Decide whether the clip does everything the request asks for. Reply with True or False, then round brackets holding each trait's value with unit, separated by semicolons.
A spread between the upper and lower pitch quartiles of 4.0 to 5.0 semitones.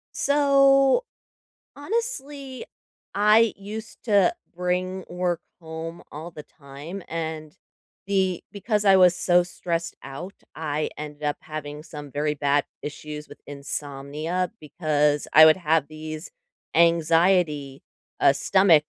True (4.3 semitones)